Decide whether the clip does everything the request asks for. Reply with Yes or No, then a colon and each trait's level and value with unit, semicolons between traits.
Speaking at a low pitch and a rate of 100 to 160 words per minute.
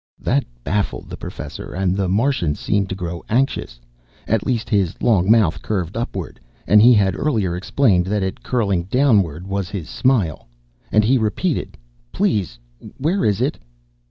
Yes: low, 100 Hz; average, 155 wpm